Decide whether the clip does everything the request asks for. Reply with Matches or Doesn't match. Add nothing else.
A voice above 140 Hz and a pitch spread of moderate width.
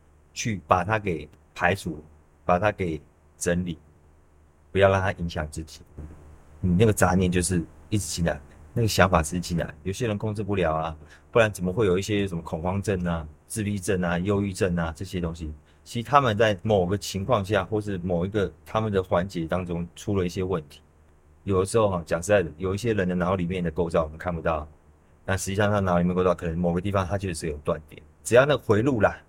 Doesn't match